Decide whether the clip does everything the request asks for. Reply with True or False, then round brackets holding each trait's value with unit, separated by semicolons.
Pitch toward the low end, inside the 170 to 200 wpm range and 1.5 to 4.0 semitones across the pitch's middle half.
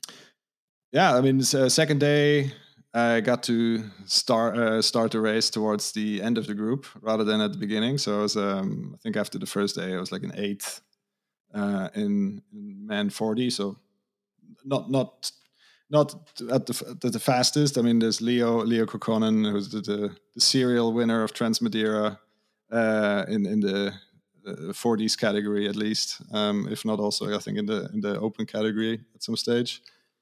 True (115 Hz; 185 wpm; 3.7 semitones)